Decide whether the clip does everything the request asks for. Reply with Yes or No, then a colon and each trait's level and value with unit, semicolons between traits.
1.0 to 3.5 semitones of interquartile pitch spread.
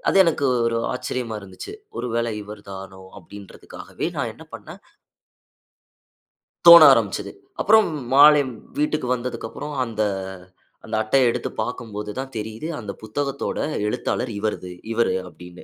No: average, 4.2 semitones